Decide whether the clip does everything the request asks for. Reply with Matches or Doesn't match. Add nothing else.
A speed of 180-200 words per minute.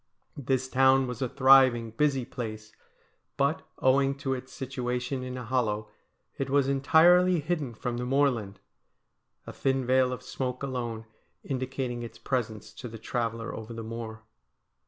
Doesn't match